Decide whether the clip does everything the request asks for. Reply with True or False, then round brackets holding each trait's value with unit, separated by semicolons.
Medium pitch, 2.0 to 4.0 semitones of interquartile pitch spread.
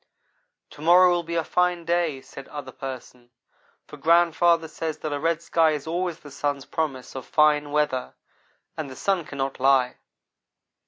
True (155 Hz; 3.6 semitones)